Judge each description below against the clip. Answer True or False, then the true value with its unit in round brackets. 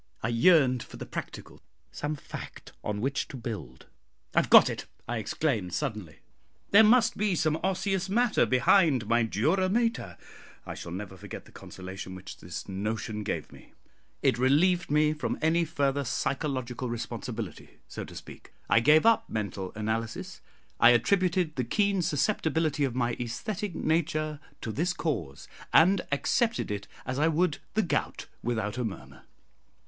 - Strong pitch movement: True (7.4 semitones)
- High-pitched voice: False (140 Hz)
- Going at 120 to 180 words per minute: True (155 wpm)